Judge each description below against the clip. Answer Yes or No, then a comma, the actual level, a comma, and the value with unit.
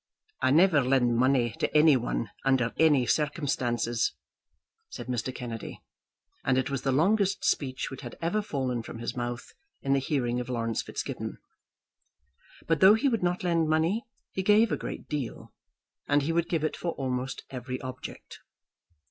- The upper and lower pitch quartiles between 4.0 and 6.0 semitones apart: Yes, average, 4.7 semitones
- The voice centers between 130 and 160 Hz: Yes, low, 135 Hz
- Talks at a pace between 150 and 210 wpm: Yes, average, 165 wpm